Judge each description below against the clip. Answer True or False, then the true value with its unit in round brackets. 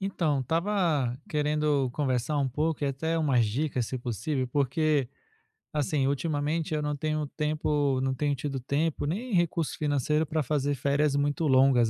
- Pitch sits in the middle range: True (145 Hz)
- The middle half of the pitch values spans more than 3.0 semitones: False (2.5 semitones)